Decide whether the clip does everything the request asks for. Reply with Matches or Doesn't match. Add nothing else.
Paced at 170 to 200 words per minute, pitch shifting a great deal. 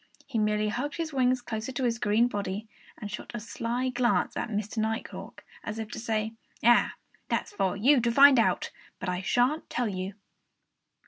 Doesn't match